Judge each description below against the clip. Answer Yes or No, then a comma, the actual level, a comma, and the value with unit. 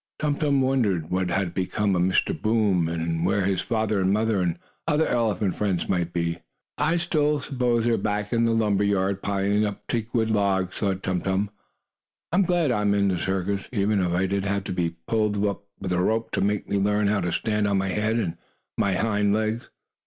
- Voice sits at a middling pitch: No, low, 100 Hz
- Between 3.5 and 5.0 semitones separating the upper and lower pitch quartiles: No, average, 2.9 semitones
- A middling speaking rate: No, fast, 220 wpm